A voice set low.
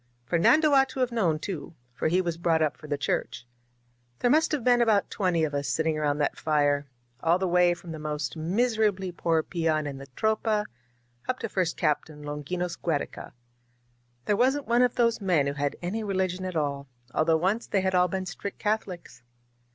No: medium, 175 Hz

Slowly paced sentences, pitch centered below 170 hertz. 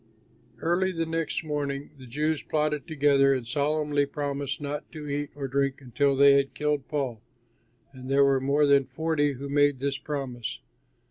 No: average, 165 wpm; medium, 140 Hz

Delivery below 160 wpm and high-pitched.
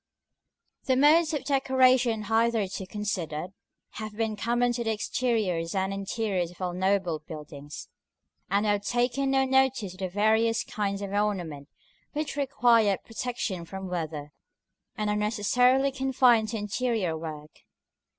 Yes: average, 145 wpm; high, 210 Hz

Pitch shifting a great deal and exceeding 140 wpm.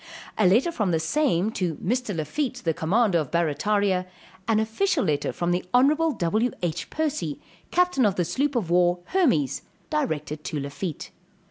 Yes: wide, 7.3 semitones; average, 155 wpm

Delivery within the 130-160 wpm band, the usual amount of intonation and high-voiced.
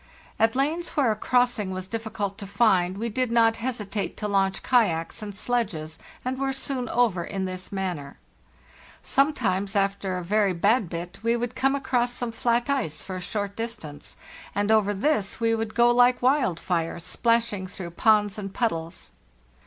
No: average, 170 wpm; average, 4.2 semitones; high, 215 Hz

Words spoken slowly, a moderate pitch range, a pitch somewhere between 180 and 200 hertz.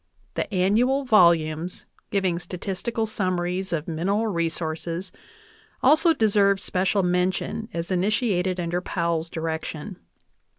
Yes: slow, 100 wpm; average, 3.3 semitones; medium, 185 Hz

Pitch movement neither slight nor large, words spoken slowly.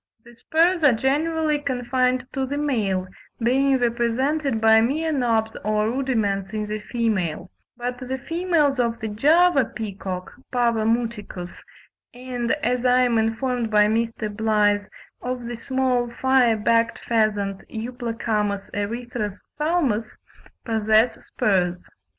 Yes: average, 3.3 semitones; slow, 120 wpm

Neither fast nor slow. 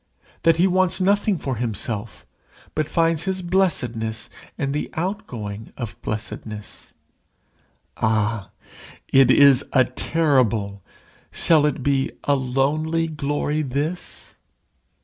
No: slow, 110 wpm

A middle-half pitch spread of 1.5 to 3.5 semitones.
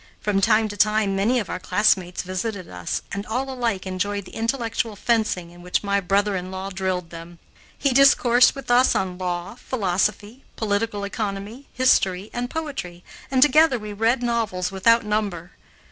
No: average, 4.0 semitones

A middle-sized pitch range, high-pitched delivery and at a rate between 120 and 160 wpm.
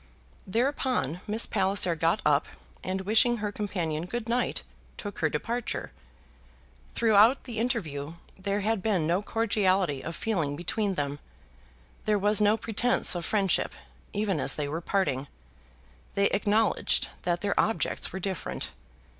Yes: average, 4.7 semitones; high, 200 Hz; average, 140 wpm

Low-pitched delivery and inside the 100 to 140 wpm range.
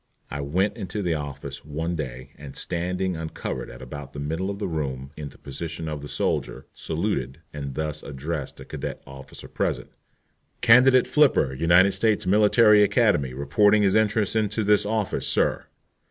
No: very low, 85 Hz; average, 165 wpm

